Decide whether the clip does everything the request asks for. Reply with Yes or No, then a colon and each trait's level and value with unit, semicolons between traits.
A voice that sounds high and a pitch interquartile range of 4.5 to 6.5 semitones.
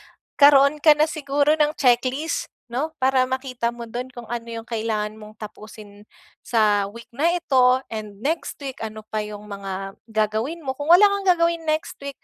Yes: very high, 250 Hz; wide, 5.4 semitones